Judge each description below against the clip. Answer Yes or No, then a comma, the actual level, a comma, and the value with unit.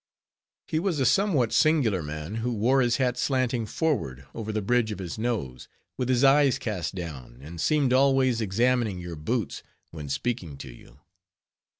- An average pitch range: No, wide, 7.0 semitones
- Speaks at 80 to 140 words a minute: No, average, 170 wpm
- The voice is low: Yes, low, 115 Hz